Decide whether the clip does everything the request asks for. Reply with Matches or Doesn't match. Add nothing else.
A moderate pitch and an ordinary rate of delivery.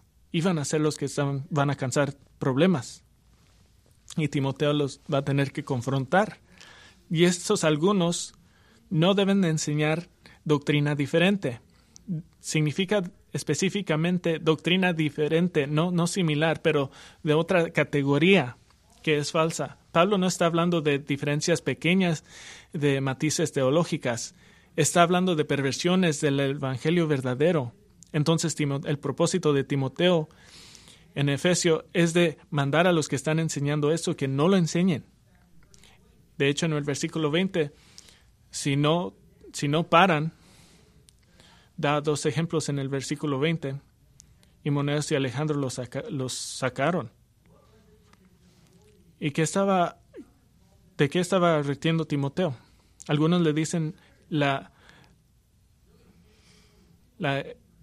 Doesn't match